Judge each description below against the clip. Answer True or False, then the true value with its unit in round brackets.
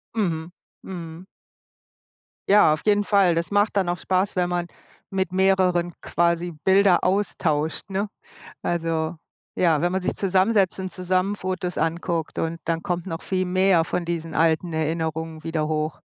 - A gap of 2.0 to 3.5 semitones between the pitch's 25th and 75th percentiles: True (2.5 semitones)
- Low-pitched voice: False (175 Hz)